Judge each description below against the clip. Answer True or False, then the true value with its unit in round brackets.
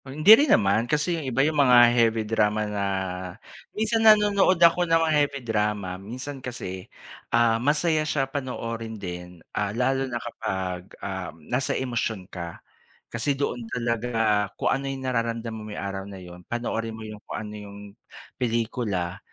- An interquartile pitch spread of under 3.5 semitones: False (4.6 semitones)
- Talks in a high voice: False (115 Hz)